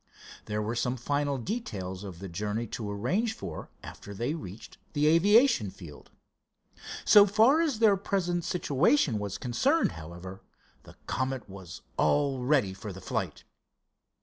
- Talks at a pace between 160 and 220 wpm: No, average, 145 wpm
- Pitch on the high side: No, low, 125 Hz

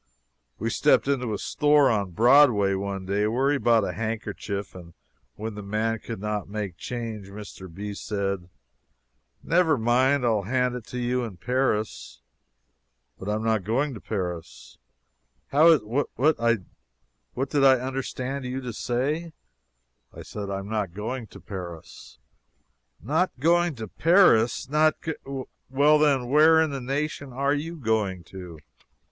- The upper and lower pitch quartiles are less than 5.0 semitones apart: No, average, 5.3 semitones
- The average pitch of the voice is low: Yes, low, 115 Hz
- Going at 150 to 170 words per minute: Yes, average, 155 wpm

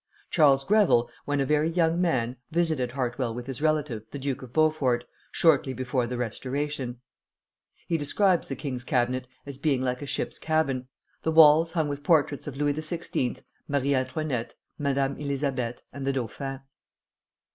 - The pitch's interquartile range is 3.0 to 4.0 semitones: Yes, average, 3.4 semitones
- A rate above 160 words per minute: No, average, 155 wpm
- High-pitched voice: No, medium, 140 Hz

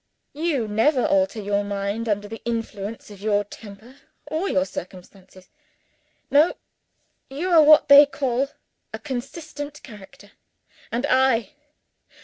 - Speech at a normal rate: No, slow, 125 wpm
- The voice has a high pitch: Yes, high, 235 Hz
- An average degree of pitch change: No, wide, 5.9 semitones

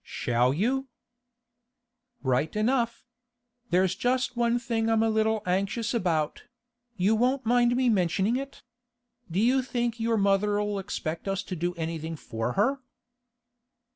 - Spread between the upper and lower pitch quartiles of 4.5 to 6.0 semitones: Yes, average, 5.0 semitones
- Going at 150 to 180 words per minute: No, slow, 135 wpm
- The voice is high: Yes, high, 215 Hz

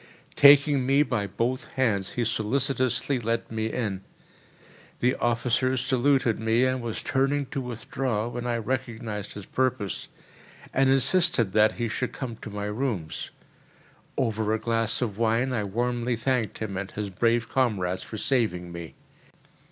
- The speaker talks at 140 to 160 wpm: Yes, average, 150 wpm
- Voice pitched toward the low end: Yes, low, 115 Hz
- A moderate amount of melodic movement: Yes, average, 3.2 semitones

